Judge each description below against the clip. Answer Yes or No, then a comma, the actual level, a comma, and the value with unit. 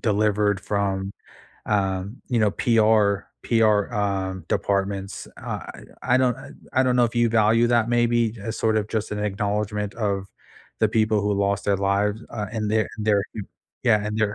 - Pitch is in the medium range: No, low, 105 Hz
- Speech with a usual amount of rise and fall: No, narrow, 2.0 semitones